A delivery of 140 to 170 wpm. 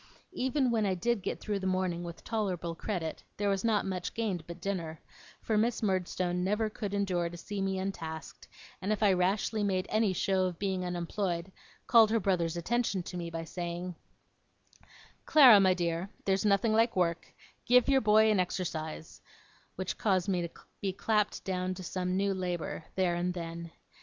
No: average, 180 wpm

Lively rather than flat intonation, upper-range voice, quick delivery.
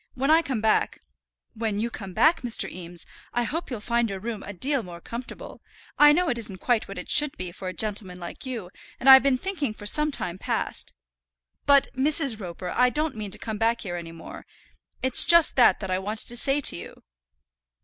Yes: wide, 6.1 semitones; high, 230 Hz; fast, 220 wpm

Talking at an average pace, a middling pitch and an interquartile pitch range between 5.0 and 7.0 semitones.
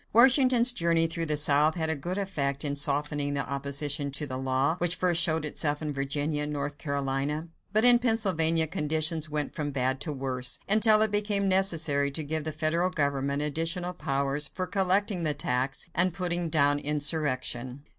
No: average, 175 wpm; medium, 150 Hz; average, 3.7 semitones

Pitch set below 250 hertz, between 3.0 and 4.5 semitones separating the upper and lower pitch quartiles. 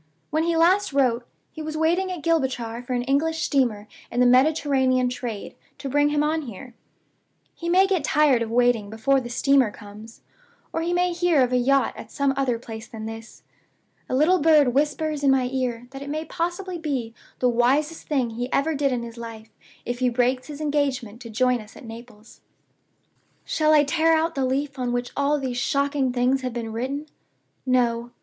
No: very high, 265 Hz; average, 3.9 semitones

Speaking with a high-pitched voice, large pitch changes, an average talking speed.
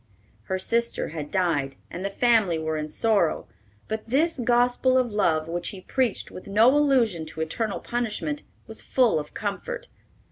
Yes: high, 215 Hz; wide, 6.3 semitones; average, 165 wpm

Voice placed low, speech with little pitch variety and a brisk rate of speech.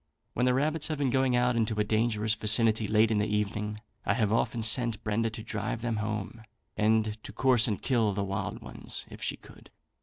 Yes: low, 110 Hz; narrow, 2.1 semitones; fast, 210 wpm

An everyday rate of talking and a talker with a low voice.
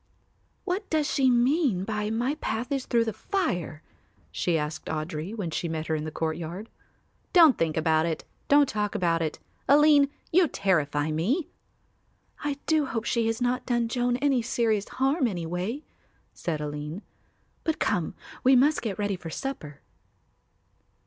No: average, 155 wpm; high, 220 Hz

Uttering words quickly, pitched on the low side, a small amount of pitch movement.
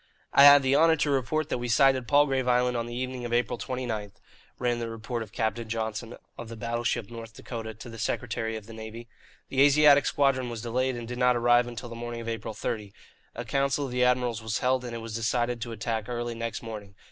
Yes: fast, 230 wpm; low, 120 Hz; narrow, 2.0 semitones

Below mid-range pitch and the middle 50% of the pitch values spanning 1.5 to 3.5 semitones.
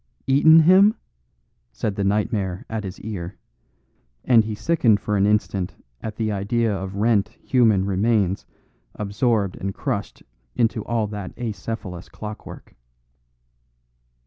Yes: low, 105 Hz; average, 2.7 semitones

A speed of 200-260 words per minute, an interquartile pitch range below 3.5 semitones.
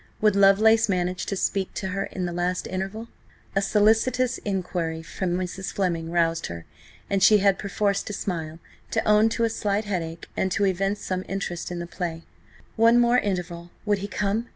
No: average, 180 wpm; average, 3.0 semitones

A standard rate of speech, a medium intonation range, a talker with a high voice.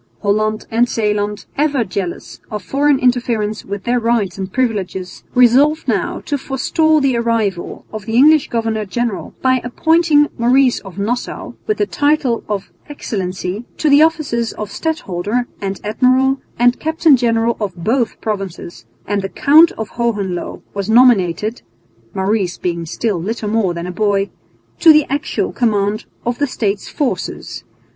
Yes: average, 150 wpm; average, 4.6 semitones; high, 230 Hz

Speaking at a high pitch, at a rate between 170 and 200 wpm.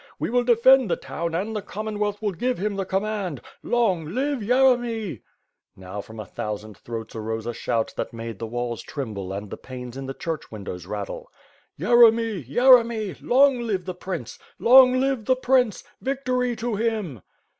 Yes: high, 205 Hz; average, 175 wpm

